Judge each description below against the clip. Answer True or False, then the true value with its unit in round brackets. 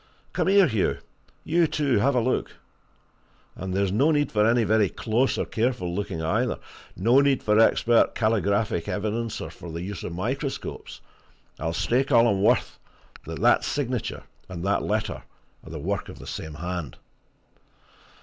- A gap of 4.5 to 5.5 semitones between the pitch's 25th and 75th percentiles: True (5.1 semitones)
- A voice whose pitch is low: True (110 Hz)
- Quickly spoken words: False (165 wpm)